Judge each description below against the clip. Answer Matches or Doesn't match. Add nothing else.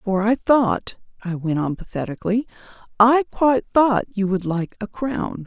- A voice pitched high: Matches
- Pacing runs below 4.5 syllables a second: Doesn't match